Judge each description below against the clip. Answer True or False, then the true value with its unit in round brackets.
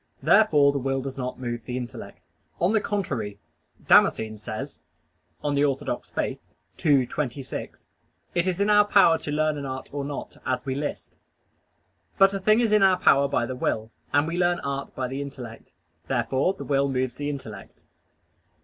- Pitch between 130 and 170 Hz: True (140 Hz)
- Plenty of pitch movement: False (5.0 semitones)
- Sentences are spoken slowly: False (175 wpm)